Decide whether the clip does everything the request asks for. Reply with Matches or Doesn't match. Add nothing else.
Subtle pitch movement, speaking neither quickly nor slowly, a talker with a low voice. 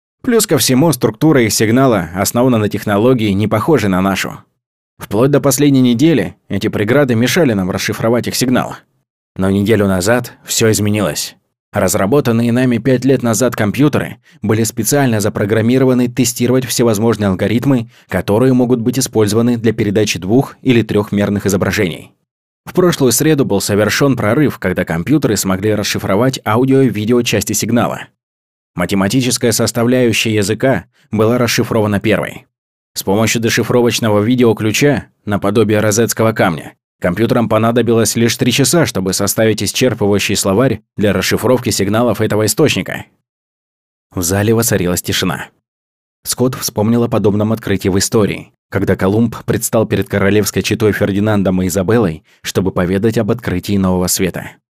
Doesn't match